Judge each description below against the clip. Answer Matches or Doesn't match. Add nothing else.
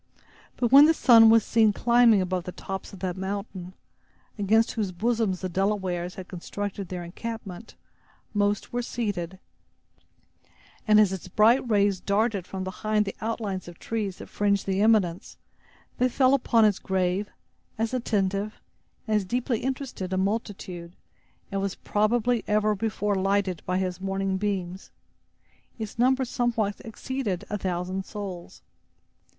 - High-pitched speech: Matches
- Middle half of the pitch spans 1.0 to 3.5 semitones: Matches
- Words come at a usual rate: Matches